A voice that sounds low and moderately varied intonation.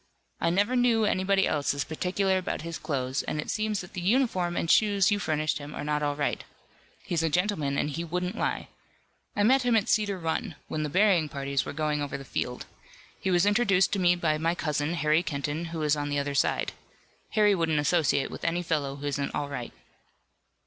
No: medium, 165 Hz; average, 4.7 semitones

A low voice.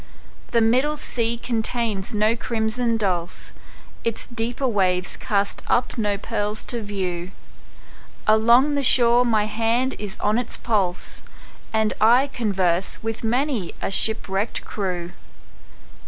No: high, 220 Hz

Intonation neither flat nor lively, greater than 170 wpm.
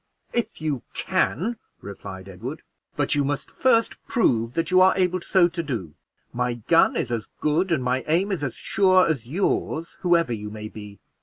No: wide, 7.6 semitones; average, 180 wpm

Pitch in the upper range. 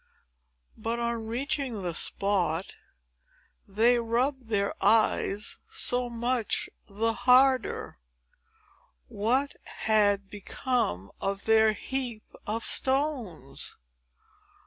Yes: high, 225 Hz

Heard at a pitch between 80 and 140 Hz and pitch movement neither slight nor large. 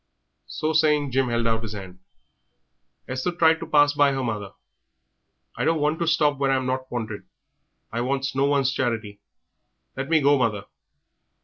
Yes: low, 135 Hz; average, 3.9 semitones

